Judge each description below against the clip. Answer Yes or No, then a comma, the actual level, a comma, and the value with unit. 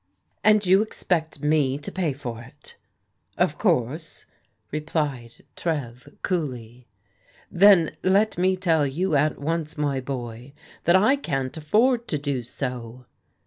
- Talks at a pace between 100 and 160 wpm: Yes, average, 140 wpm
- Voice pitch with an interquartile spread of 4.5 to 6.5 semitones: Yes, wide, 5.6 semitones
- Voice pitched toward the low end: No, medium, 150 Hz